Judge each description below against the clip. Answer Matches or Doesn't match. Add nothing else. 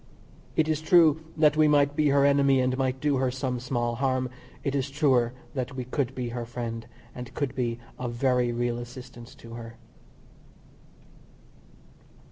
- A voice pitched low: Matches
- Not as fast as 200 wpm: Matches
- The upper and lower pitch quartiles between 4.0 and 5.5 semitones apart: Doesn't match